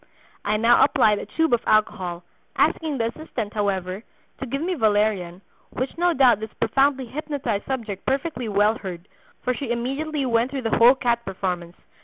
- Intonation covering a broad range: No, average, 4.7 semitones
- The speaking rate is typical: Yes, average, 170 wpm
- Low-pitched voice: No, high, 230 Hz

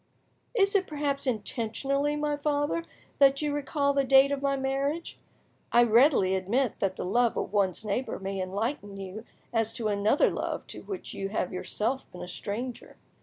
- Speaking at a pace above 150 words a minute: Yes, average, 170 wpm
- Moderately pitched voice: No, very high, 255 Hz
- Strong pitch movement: Yes, wide, 5.7 semitones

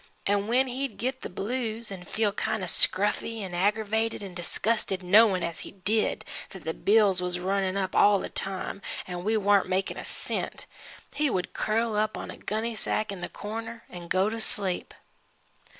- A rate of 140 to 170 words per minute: No, average, 185 wpm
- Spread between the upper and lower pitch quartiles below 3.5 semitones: Yes, average, 3.0 semitones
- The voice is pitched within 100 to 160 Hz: No, high, 205 Hz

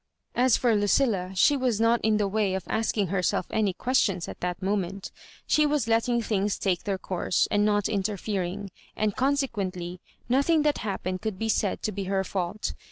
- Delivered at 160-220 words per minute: Yes, average, 180 wpm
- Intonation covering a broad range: No, average, 3.2 semitones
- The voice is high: Yes, high, 205 Hz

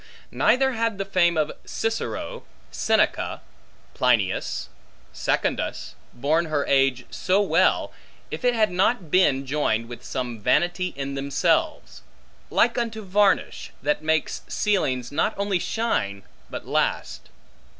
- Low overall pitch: No, medium, 165 Hz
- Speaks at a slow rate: Yes, slow, 120 wpm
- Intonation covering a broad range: Yes, wide, 7.3 semitones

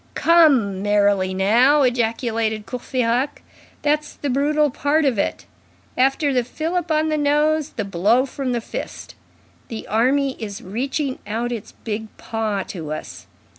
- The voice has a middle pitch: No, high, 245 Hz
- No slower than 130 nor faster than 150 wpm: Yes, average, 140 wpm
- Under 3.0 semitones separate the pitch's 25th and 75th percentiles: No, average, 5.2 semitones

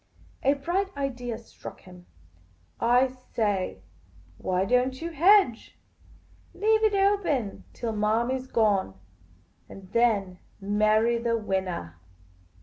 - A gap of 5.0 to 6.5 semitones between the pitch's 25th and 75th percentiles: Yes, average, 5.3 semitones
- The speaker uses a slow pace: Yes, slow, 115 wpm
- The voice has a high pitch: Yes, high, 230 Hz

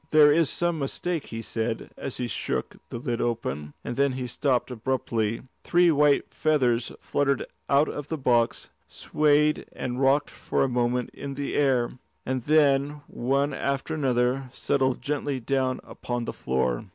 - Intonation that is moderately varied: Yes, average, 3.1 semitones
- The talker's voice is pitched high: No, low, 135 Hz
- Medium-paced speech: Yes, average, 160 wpm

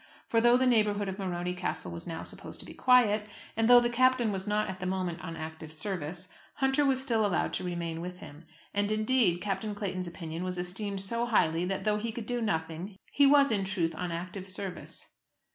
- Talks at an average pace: No, fast, 210 wpm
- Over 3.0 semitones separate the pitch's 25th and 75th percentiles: Yes, average, 4.3 semitones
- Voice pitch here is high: Yes, high, 195 Hz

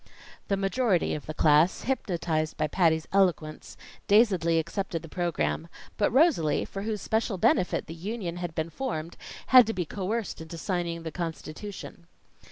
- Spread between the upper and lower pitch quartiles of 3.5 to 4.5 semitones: Yes, average, 4.0 semitones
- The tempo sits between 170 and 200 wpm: No, average, 155 wpm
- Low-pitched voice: No, medium, 175 Hz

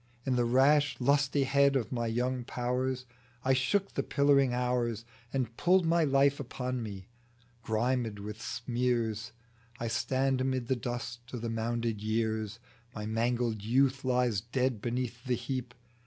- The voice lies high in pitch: No, low, 125 Hz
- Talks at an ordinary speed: Yes, average, 145 wpm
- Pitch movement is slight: Yes, narrow, 2.3 semitones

